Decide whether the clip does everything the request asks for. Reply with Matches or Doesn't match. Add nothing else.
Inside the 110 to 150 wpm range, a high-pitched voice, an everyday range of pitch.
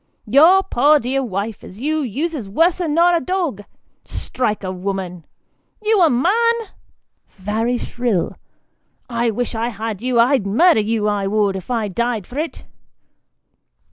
Doesn't match